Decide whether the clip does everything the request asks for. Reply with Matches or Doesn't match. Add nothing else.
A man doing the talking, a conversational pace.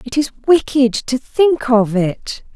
Doesn't match